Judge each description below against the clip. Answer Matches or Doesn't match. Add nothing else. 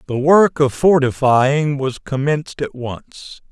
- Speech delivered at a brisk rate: Doesn't match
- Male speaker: Matches